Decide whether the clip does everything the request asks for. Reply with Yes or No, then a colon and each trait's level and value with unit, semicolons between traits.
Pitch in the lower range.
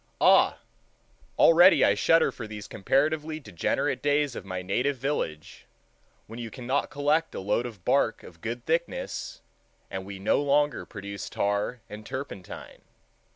Yes: low, 120 Hz